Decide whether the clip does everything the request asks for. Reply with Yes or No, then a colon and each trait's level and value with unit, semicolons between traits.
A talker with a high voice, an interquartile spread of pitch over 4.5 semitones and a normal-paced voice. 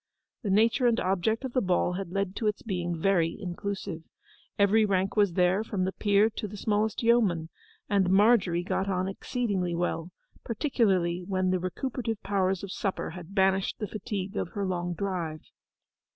No: high, 195 Hz; average, 2.7 semitones; average, 170 wpm